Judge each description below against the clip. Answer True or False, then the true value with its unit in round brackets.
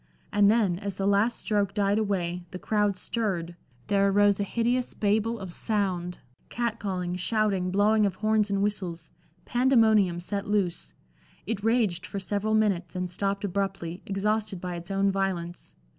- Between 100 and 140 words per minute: False (160 wpm)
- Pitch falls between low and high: False (200 Hz)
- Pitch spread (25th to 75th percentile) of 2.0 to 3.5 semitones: True (2.7 semitones)